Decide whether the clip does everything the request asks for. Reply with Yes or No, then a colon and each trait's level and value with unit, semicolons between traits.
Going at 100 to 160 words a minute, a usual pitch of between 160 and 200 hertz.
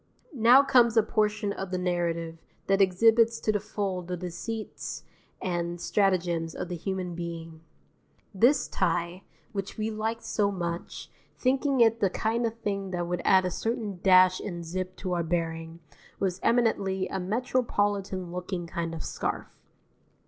Yes: average, 155 wpm; high, 190 Hz